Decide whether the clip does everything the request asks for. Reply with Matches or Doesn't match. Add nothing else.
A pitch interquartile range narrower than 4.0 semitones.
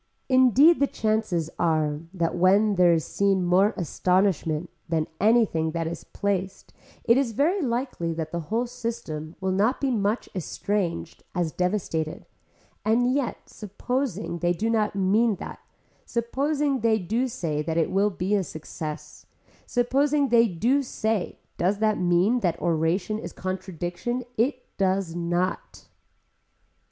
Doesn't match